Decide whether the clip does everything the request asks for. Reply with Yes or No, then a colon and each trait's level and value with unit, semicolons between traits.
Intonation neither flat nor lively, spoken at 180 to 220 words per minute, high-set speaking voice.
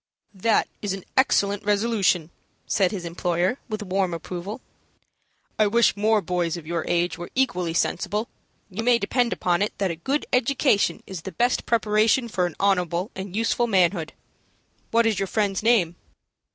No: average, 4.2 semitones; average, 165 wpm; high, 200 Hz